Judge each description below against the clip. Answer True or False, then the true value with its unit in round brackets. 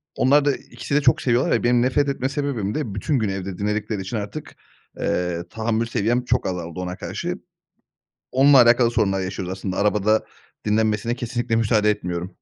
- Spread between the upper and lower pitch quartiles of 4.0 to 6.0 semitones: True (4.3 semitones)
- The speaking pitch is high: False (110 Hz)